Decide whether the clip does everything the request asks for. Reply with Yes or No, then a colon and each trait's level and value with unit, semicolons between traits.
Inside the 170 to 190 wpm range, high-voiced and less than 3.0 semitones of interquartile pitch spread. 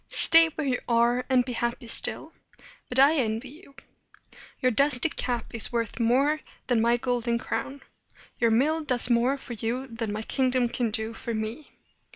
Yes: average, 175 wpm; high, 245 Hz; narrow, 2.5 semitones